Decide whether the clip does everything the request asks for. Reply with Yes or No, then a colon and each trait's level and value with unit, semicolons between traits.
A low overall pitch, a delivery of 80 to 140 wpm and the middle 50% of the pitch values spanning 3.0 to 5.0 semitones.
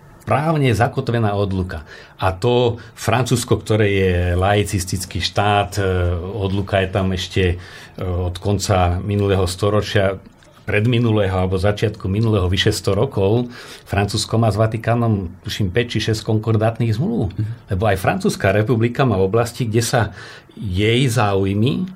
Yes: low, 105 Hz; average, 130 wpm; average, 3.3 semitones